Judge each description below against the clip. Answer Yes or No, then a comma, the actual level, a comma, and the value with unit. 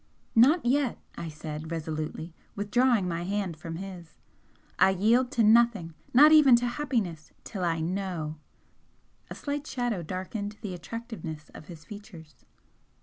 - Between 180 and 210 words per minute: No, average, 140 wpm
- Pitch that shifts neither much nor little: No, wide, 6.3 semitones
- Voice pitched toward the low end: No, high, 195 Hz